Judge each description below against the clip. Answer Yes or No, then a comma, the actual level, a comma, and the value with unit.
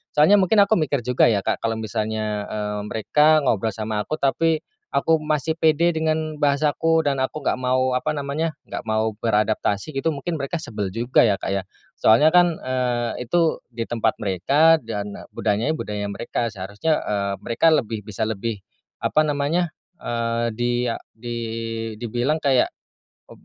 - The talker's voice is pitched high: No, low, 125 Hz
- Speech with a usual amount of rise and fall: No, wide, 6.0 semitones